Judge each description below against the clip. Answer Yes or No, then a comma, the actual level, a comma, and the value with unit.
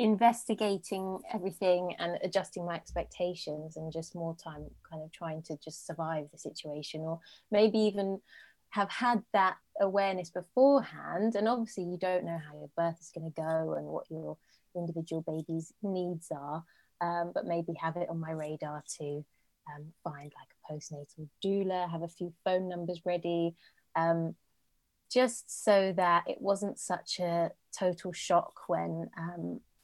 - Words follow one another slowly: No, average, 155 wpm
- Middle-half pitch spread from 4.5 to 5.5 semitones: No, average, 3.1 semitones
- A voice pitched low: No, medium, 170 Hz